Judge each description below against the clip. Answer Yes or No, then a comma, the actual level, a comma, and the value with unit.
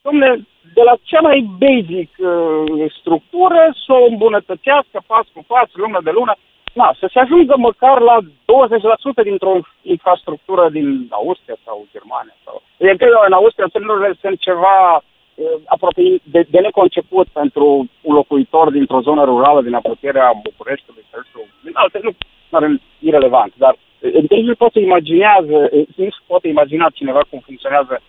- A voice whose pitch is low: No, high, 195 Hz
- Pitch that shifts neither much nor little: No, wide, 8.4 semitones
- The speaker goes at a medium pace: Yes, average, 145 wpm